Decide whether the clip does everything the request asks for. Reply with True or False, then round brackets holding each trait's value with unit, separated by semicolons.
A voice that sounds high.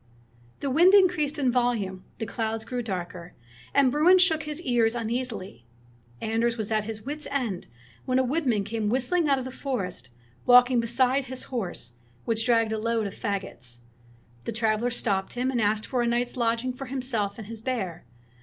True (235 Hz)